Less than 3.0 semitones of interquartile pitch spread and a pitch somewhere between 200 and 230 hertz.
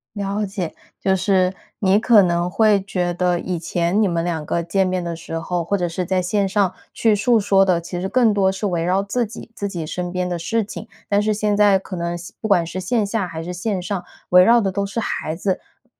No: narrow, 2.6 semitones; high, 190 Hz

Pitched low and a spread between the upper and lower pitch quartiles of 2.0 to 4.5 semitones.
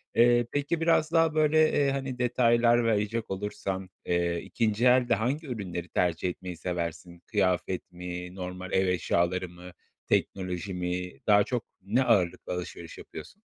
No: very low, 95 Hz; average, 5.3 semitones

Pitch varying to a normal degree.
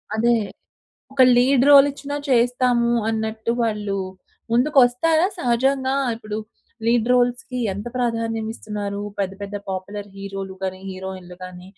Yes: average, 3.7 semitones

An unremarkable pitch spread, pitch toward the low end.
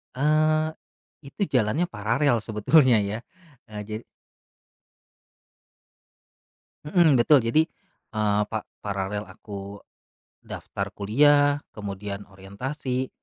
No: wide, 6.0 semitones; low, 115 Hz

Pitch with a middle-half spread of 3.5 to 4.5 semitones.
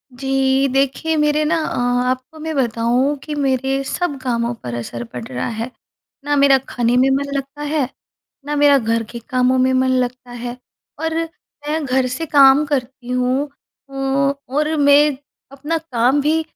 No: average, 2.7 semitones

